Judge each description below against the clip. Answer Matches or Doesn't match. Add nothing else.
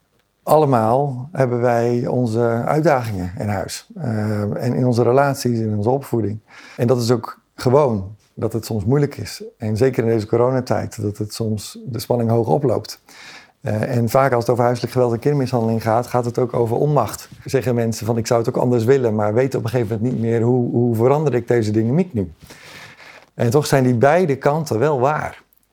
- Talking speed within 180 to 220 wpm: Matches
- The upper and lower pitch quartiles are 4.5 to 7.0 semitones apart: Doesn't match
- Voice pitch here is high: Doesn't match